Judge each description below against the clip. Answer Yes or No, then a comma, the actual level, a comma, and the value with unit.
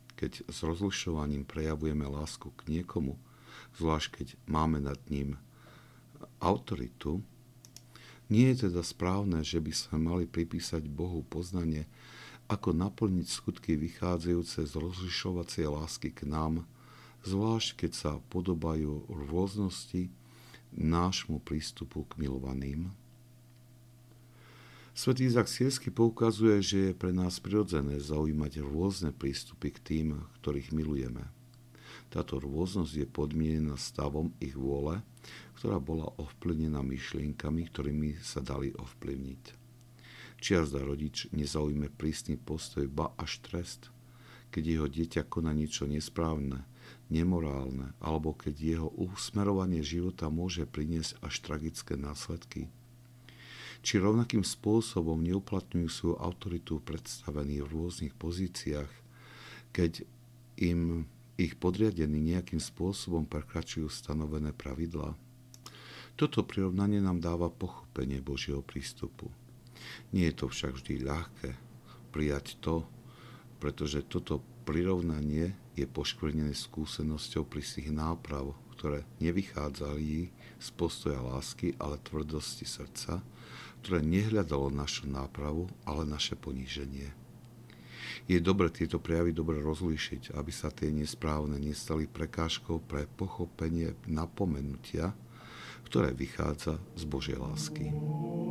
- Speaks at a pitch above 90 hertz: No, very low, 80 Hz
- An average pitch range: Yes, average, 4.6 semitones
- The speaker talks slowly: Yes, slow, 105 wpm